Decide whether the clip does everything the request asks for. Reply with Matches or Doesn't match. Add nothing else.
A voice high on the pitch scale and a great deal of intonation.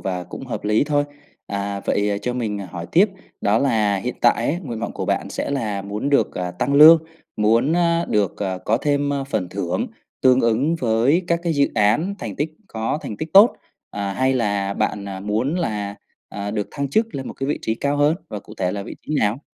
Doesn't match